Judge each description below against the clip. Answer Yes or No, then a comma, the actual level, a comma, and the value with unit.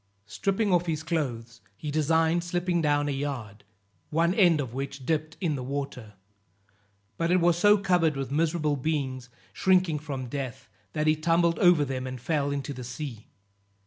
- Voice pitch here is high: No, medium, 150 Hz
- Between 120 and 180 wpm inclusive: Yes, average, 170 wpm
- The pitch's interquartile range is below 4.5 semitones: Yes, average, 4.0 semitones